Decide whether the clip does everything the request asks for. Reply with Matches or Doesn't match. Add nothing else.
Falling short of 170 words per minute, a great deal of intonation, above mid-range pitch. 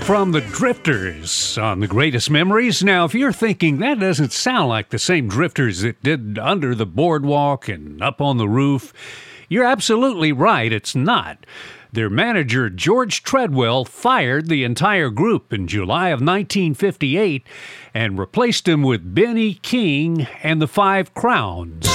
Doesn't match